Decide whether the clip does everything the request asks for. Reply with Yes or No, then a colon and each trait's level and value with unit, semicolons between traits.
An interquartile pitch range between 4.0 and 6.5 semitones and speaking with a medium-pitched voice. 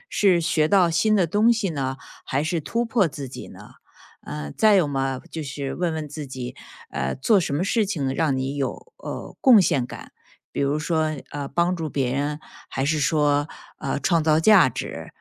Yes: average, 4.5 semitones; medium, 155 Hz